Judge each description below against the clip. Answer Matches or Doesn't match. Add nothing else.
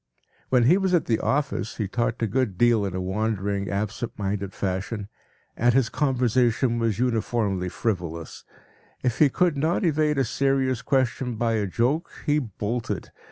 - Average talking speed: Matches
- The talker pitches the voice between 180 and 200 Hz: Doesn't match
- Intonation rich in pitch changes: Doesn't match